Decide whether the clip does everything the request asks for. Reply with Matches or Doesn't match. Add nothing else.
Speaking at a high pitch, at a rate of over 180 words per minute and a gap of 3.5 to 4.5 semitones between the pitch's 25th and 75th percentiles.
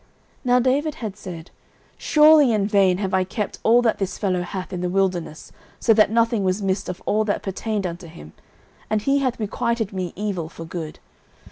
Matches